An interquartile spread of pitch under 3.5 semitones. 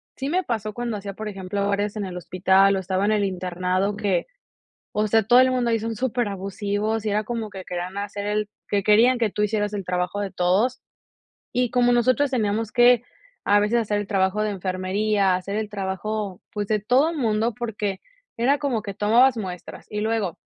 Yes: narrow, 2.6 semitones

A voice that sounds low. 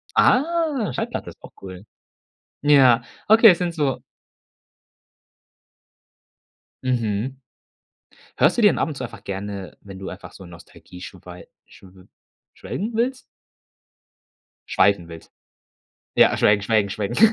Yes: low, 115 Hz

